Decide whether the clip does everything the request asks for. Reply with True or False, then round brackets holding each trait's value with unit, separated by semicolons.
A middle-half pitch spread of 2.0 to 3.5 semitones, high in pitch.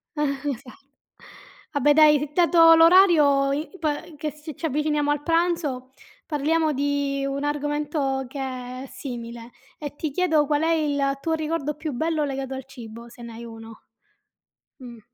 True (2.6 semitones; 290 Hz)